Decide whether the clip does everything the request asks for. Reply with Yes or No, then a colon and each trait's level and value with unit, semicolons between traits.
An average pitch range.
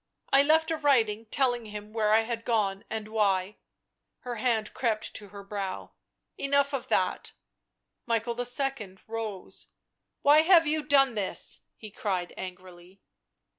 Yes: average, 4.8 semitones